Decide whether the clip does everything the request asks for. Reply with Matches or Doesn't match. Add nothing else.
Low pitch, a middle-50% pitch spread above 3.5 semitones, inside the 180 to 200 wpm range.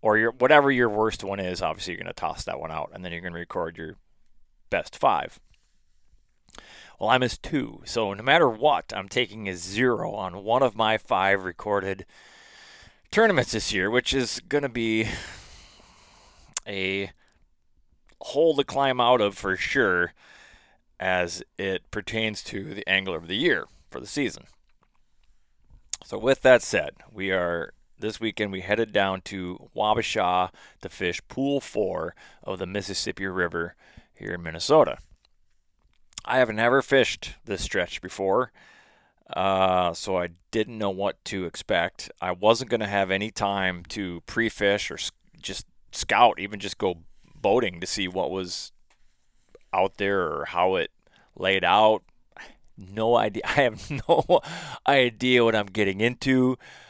Doesn't match